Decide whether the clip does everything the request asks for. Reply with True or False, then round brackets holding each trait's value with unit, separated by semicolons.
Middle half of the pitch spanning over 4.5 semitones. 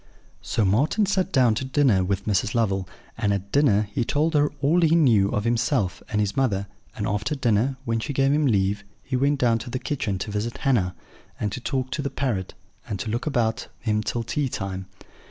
True (5.2 semitones)